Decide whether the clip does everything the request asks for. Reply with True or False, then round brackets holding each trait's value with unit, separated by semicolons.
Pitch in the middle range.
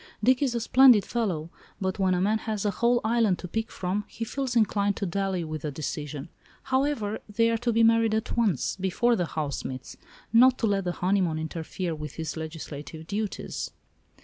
False (200 Hz)